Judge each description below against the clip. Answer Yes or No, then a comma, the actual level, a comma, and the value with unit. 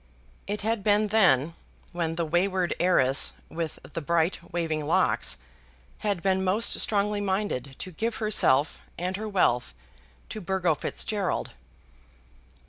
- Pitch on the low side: No, medium, 185 Hz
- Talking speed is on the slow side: Yes, slow, 130 wpm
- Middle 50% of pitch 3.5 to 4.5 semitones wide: Yes, average, 4.0 semitones